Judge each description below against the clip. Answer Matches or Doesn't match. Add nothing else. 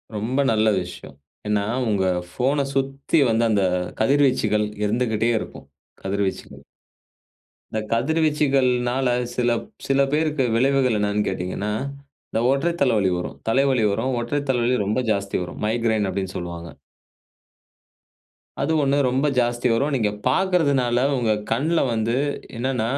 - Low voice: Matches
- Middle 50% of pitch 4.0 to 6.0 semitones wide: Matches